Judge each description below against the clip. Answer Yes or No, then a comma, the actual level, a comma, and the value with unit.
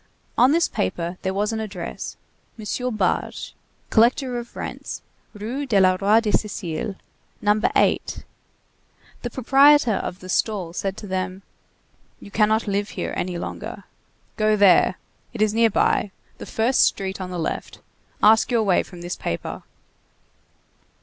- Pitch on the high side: Yes, high, 210 Hz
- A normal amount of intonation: Yes, average, 3.2 semitones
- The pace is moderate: Yes, average, 145 wpm